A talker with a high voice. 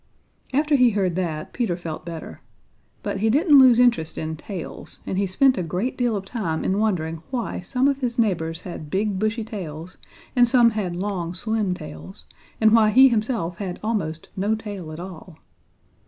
Yes: high, 200 Hz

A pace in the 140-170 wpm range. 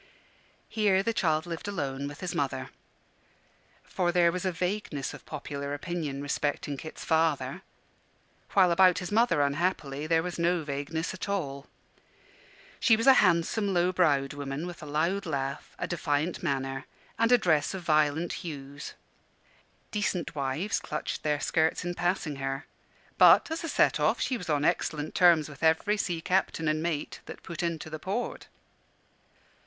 Yes: average, 160 wpm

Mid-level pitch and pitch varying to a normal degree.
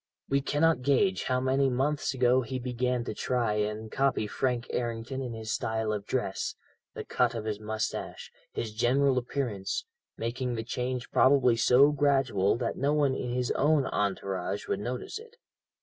No: low, 125 Hz; average, 3.2 semitones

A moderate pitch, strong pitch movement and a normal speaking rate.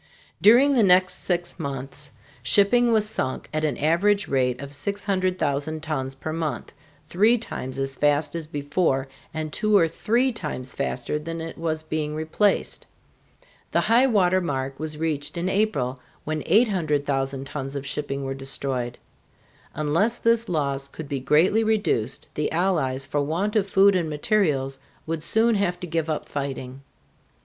Yes: medium, 155 Hz; wide, 5.7 semitones; average, 155 wpm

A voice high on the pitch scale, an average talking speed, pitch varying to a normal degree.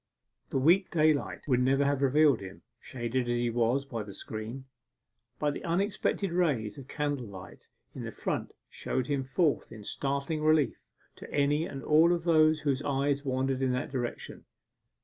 No: medium, 140 Hz; average, 170 wpm; average, 3.4 semitones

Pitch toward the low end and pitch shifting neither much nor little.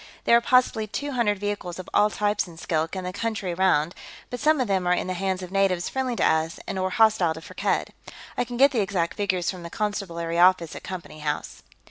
No: high, 190 Hz; average, 3.7 semitones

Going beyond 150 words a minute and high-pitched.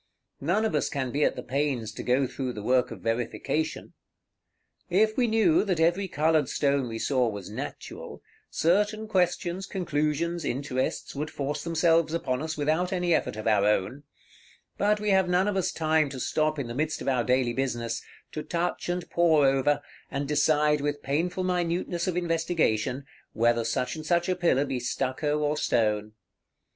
No: average, 175 wpm; medium, 150 Hz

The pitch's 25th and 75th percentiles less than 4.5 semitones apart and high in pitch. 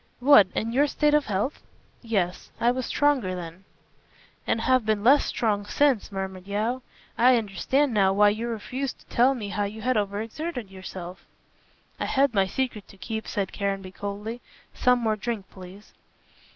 Yes: average, 4.1 semitones; high, 215 Hz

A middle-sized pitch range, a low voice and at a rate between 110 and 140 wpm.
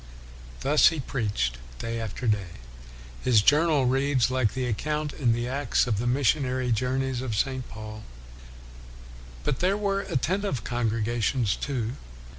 Yes: average, 3.6 semitones; low, 125 Hz; slow, 135 wpm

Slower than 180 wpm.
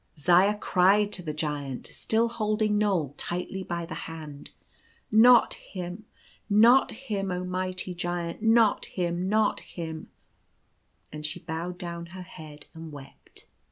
Yes: average, 150 wpm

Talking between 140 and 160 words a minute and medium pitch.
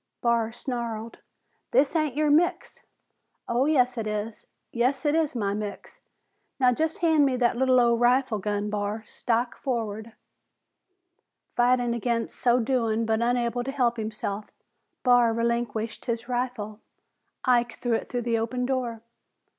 No: average, 145 wpm; high, 240 Hz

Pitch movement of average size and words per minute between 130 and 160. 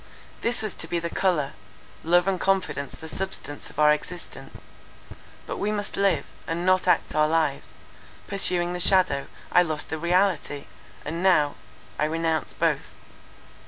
Yes: average, 3.4 semitones; average, 145 wpm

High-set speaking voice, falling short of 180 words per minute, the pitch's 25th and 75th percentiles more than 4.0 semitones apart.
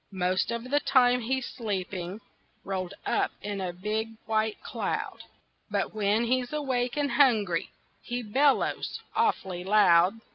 Yes: high, 220 Hz; slow, 135 wpm; average, 4.4 semitones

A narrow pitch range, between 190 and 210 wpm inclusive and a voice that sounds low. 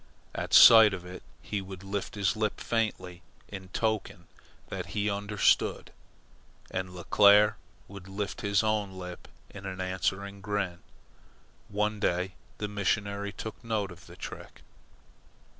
No: narrow, 2.0 semitones; slow, 135 wpm; low, 100 Hz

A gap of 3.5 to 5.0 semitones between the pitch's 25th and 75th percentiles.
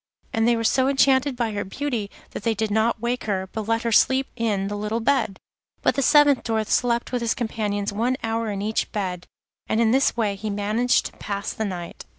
No: average, 2.8 semitones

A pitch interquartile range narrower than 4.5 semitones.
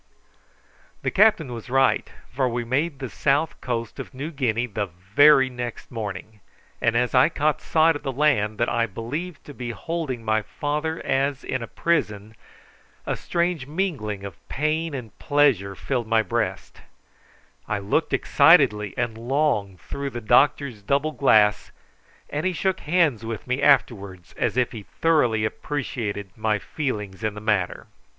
No: wide, 5.4 semitones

